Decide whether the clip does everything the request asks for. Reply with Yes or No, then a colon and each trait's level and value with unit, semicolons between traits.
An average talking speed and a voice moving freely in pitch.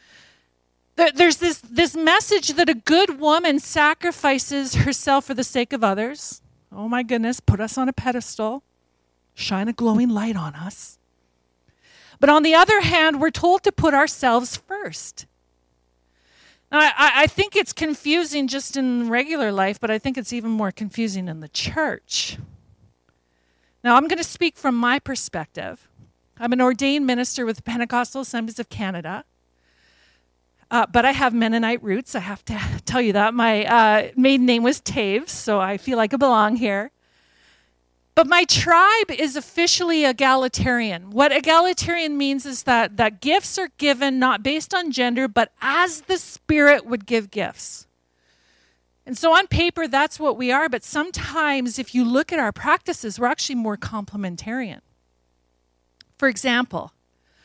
Yes: average, 160 wpm; wide, 6.7 semitones